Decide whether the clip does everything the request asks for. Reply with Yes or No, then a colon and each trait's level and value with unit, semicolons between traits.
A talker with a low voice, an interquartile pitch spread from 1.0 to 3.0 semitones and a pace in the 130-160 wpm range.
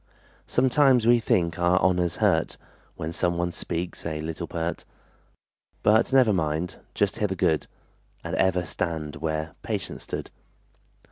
Yes: very low, 85 Hz; average, 2.7 semitones; average, 140 wpm